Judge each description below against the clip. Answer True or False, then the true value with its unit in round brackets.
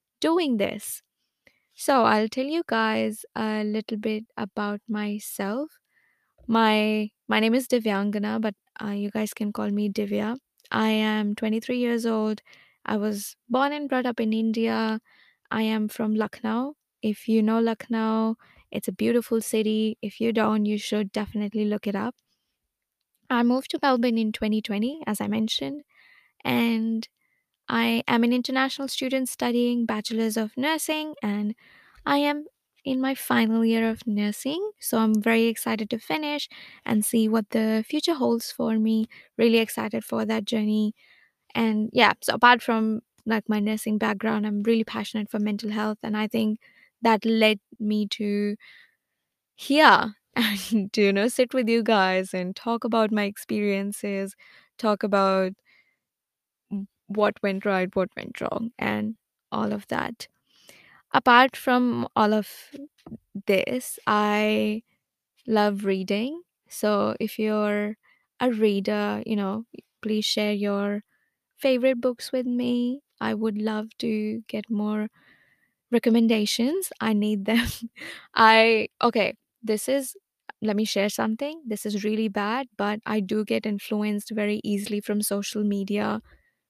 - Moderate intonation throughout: False (2.0 semitones)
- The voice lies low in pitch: False (220 Hz)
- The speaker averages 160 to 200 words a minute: False (145 wpm)